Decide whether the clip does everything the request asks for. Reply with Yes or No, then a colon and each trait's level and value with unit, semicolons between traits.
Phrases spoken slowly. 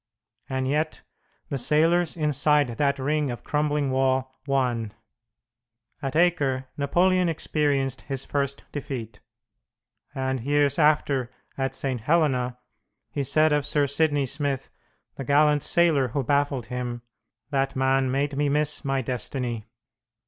Yes: slow, 125 wpm